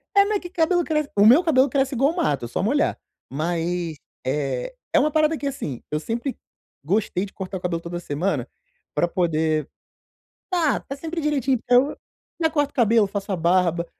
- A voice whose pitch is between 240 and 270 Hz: No, high, 225 Hz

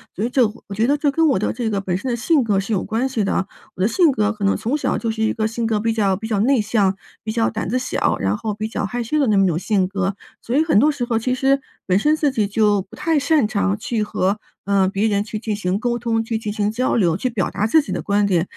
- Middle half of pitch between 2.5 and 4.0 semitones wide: Yes, average, 3.5 semitones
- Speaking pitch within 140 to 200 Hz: No, high, 220 Hz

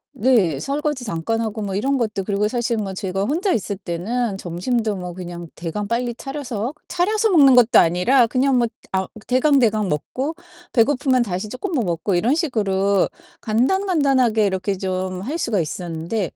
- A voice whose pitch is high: Yes, high, 220 Hz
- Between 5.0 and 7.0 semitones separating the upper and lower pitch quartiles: Yes, wide, 5.5 semitones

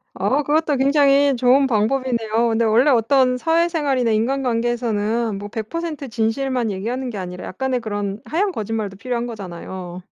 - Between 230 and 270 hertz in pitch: Yes, high, 240 Hz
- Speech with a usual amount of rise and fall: Yes, average, 3.9 semitones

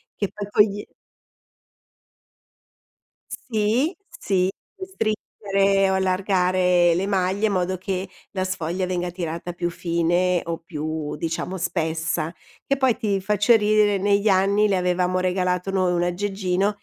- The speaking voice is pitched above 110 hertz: Yes, medium, 185 Hz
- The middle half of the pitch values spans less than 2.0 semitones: No, narrow, 2.4 semitones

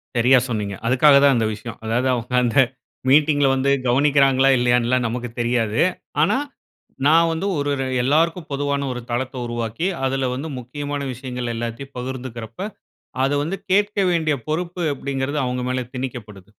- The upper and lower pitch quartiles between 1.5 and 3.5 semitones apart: Yes, average, 3.1 semitones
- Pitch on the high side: No, low, 130 Hz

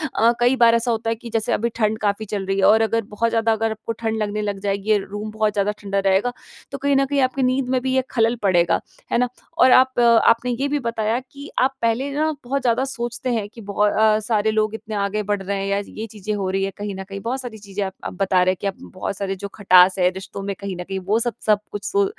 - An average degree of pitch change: Yes, average, 3.1 semitones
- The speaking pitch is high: Yes, high, 215 Hz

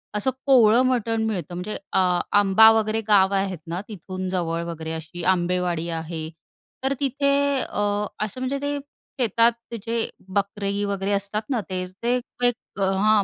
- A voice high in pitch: Yes, high, 200 Hz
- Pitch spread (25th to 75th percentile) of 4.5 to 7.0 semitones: No, average, 3.7 semitones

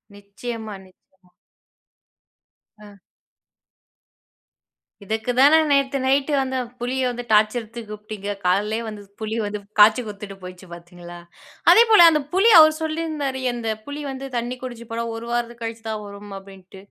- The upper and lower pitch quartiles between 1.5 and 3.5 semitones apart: No, average, 4.3 semitones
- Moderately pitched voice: No, high, 225 Hz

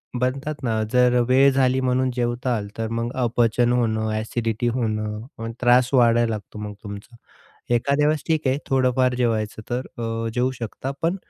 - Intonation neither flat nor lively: No, narrow, 2.2 semitones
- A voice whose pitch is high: No, low, 120 Hz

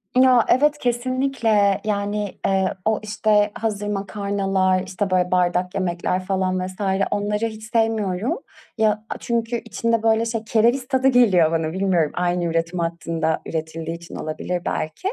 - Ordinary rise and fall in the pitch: Yes, average, 3.8 semitones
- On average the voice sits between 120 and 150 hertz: No, high, 200 Hz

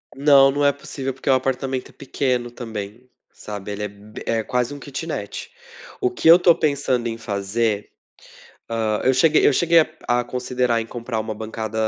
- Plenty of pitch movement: No, average, 3.9 semitones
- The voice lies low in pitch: Yes, low, 125 Hz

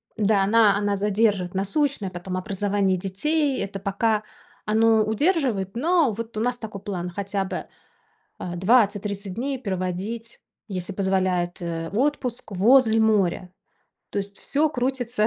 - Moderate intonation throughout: Yes, average, 3.3 semitones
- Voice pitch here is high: Yes, high, 205 Hz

